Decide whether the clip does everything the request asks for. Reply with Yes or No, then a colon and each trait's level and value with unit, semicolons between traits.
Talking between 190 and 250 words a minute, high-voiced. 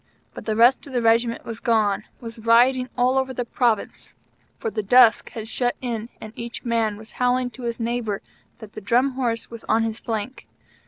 Yes: average, 200 wpm; high, 235 Hz